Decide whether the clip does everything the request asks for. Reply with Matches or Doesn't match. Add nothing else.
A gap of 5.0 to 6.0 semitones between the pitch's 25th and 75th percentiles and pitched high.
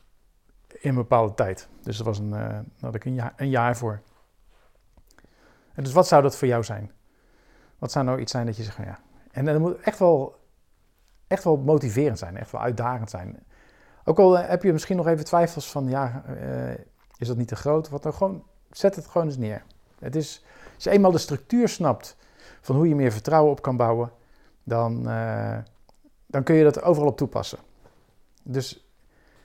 Doesn't match